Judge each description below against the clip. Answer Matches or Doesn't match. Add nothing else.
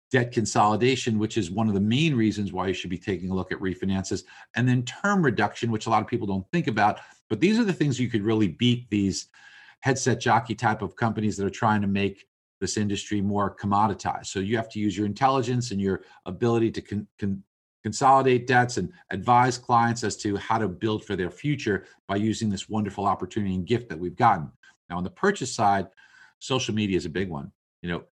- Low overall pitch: Matches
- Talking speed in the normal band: Doesn't match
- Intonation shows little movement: Doesn't match